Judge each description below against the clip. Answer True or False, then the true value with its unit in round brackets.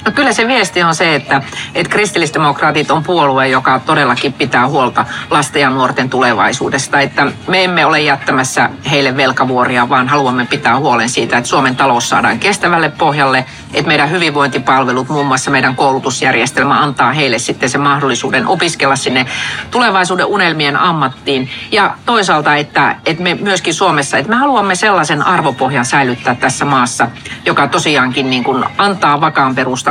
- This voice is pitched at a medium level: True (145 Hz)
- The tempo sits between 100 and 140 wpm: False (155 wpm)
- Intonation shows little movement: False (4.4 semitones)